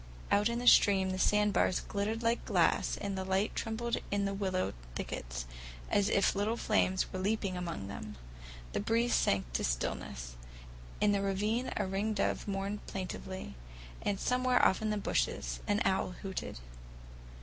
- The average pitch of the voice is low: No, high, 200 Hz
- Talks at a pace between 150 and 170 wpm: Yes, average, 160 wpm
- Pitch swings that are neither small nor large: No, narrow, 2.3 semitones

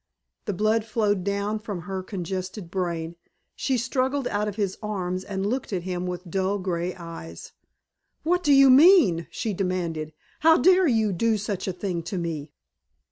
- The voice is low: No, high, 195 Hz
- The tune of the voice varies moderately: Yes, average, 3.9 semitones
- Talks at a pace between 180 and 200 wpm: No, average, 170 wpm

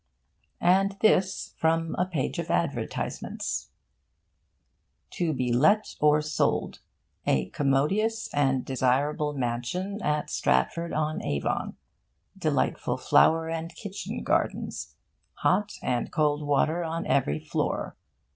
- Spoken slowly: Yes, slow, 110 wpm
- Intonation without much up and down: No, average, 4.6 semitones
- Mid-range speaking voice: Yes, medium, 150 Hz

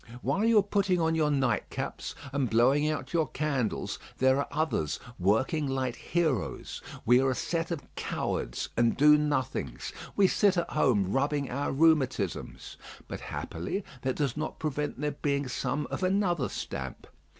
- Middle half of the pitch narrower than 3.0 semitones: No, average, 3.7 semitones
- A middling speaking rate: Yes, average, 160 wpm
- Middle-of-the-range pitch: Yes, medium, 145 Hz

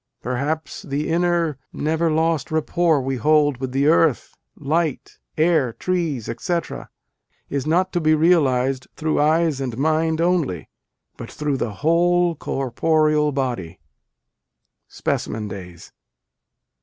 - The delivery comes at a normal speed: No, slow, 115 wpm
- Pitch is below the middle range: No, medium, 155 Hz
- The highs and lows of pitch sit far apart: No, average, 3.7 semitones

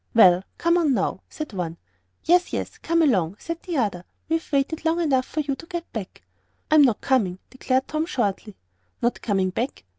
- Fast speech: No, average, 180 wpm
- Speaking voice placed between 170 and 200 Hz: No, very high, 265 Hz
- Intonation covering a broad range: Yes, wide, 8.2 semitones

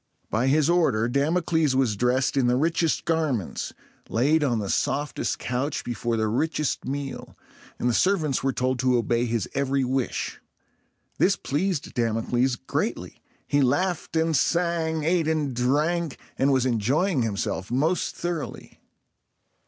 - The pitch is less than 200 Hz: Yes, low, 135 Hz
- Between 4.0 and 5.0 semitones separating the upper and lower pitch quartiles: Yes, average, 4.6 semitones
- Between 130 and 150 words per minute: Yes, average, 140 wpm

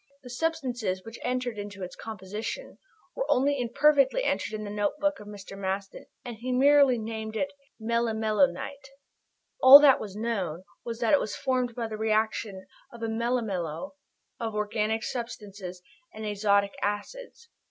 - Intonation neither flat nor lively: Yes, average, 3.5 semitones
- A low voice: No, high, 225 Hz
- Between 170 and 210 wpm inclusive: No, average, 150 wpm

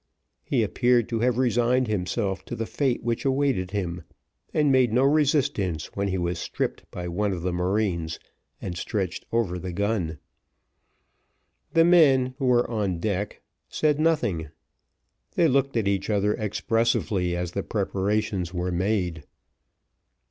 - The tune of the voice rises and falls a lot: Yes, wide, 5.7 semitones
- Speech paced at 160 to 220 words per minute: No, average, 145 wpm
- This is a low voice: Yes, low, 105 Hz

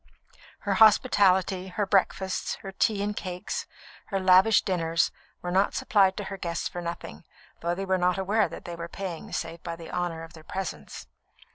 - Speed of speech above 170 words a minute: Yes, average, 180 wpm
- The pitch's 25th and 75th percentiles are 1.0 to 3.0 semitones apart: Yes, narrow, 2.4 semitones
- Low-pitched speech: No, medium, 185 Hz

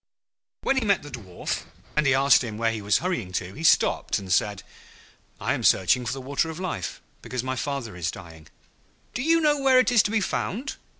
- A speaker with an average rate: No, fast, 220 wpm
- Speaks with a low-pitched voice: Yes, low, 130 Hz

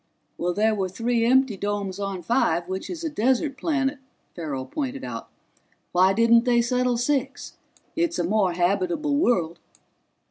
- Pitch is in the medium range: No, high, 230 Hz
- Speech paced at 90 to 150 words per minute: Yes, average, 145 wpm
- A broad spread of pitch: Yes, wide, 6.0 semitones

